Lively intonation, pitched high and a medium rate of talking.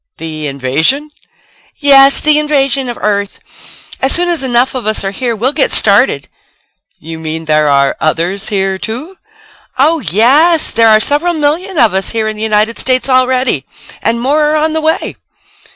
Yes: wide, 7.1 semitones; high, 240 Hz; average, 170 wpm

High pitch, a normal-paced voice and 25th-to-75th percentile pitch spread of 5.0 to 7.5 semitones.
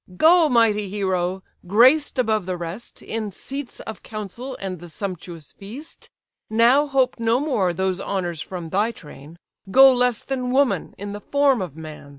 Yes: high, 210 Hz; average, 160 wpm; wide, 5.5 semitones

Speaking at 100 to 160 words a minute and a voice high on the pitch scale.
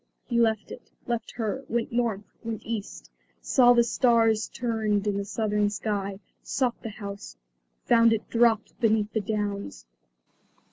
Yes: average, 145 wpm; high, 220 Hz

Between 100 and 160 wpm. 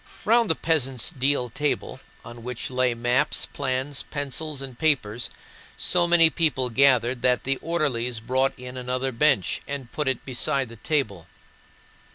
Yes: average, 150 wpm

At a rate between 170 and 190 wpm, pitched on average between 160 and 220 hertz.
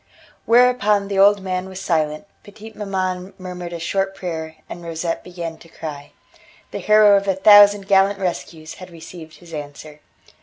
No: average, 160 wpm; medium, 185 Hz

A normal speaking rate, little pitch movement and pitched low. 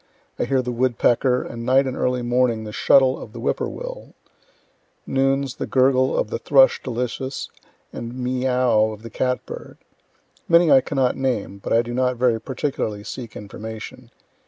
Yes: average, 175 wpm; narrow, 2.2 semitones; low, 125 Hz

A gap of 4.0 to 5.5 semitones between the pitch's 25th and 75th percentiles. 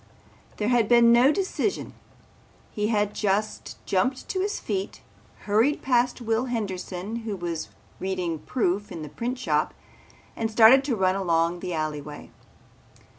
Yes: average, 4.6 semitones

